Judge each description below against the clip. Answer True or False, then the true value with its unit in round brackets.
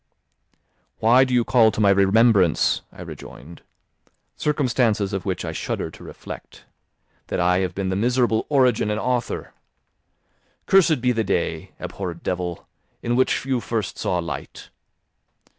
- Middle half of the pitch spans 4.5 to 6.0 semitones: True (4.9 semitones)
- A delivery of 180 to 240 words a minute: False (140 wpm)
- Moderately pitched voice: False (110 Hz)